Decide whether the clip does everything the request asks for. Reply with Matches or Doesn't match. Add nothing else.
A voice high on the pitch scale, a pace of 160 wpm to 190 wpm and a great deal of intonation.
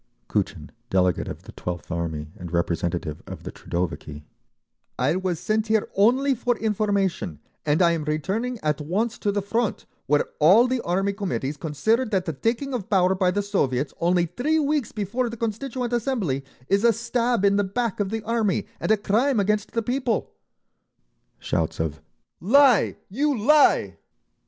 Matches